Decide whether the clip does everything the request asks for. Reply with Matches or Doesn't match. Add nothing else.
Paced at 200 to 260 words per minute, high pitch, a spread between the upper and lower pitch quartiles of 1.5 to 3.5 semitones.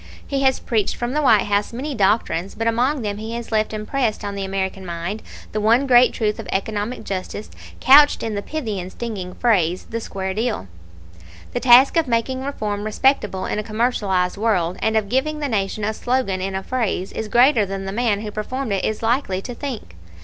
Doesn't match